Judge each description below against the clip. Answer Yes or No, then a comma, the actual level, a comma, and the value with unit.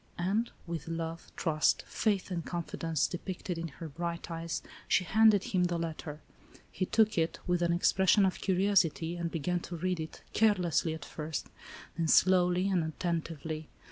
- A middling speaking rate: Yes, average, 165 wpm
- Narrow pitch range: Yes, narrow, 2.2 semitones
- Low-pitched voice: No, medium, 170 Hz